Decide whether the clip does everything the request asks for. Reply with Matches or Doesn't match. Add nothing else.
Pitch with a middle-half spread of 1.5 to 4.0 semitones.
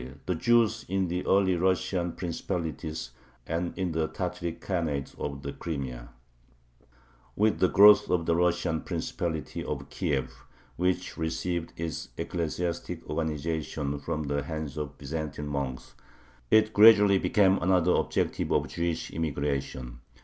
Matches